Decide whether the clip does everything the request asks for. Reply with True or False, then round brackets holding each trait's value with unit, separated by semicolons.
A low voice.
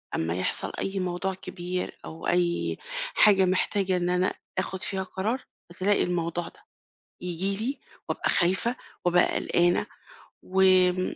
False (185 Hz)